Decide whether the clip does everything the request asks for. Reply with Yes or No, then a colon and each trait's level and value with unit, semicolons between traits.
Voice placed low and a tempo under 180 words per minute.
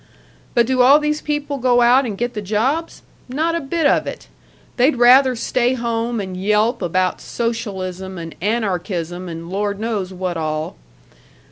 No: high, 230 Hz; average, 160 wpm